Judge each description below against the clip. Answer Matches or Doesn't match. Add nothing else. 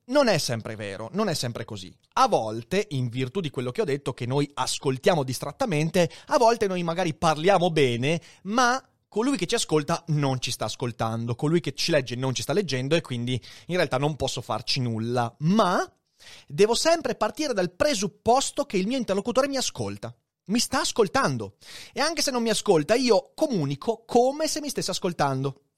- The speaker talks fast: Matches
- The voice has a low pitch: Doesn't match